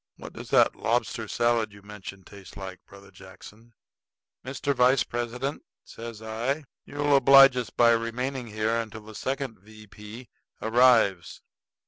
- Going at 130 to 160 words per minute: Yes, average, 140 wpm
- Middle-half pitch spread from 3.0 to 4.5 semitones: Yes, average, 3.3 semitones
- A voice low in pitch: Yes, low, 115 Hz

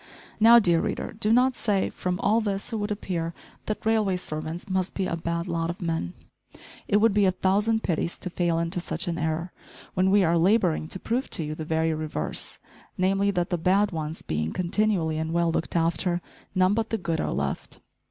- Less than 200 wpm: No, fast, 205 wpm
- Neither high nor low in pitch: Yes, medium, 180 Hz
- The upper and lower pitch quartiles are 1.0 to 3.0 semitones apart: No, average, 3.6 semitones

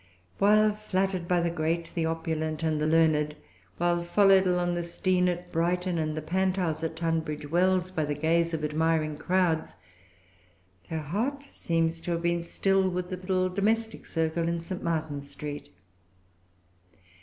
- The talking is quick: No, average, 155 wpm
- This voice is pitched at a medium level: Yes, medium, 170 Hz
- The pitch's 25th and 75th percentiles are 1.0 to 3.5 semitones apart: Yes, narrow, 2.5 semitones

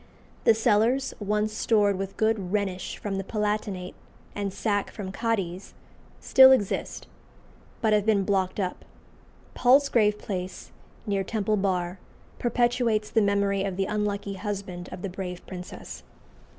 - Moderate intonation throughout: No, narrow, 2.1 semitones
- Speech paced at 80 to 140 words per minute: Yes, slow, 135 wpm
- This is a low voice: No, high, 205 Hz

